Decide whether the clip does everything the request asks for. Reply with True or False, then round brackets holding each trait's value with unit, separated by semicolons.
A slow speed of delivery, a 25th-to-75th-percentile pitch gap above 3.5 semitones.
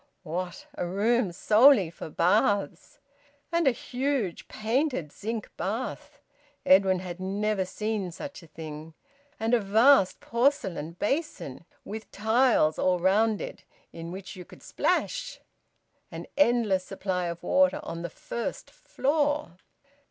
True (130 wpm; 5.4 semitones)